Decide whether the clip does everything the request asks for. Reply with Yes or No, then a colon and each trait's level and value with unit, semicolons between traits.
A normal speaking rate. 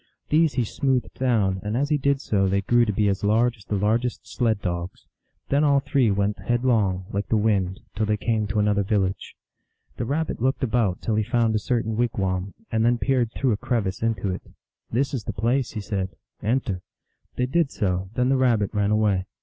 No: fast, 215 wpm